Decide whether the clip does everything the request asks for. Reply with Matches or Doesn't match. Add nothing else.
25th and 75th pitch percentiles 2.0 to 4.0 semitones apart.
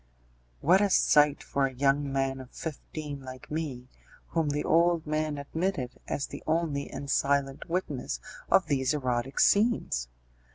Matches